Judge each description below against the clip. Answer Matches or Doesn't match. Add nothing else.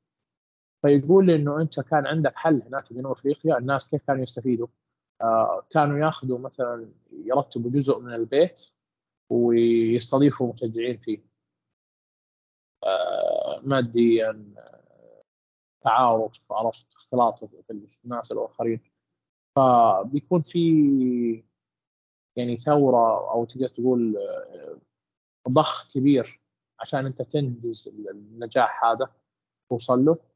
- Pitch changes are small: Doesn't match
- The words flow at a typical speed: Matches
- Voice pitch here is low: Matches